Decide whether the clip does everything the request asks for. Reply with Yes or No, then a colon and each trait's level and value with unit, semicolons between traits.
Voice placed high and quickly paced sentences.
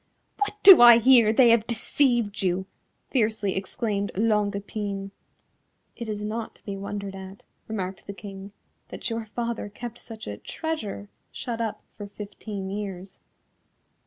No: high, 210 Hz; average, 145 wpm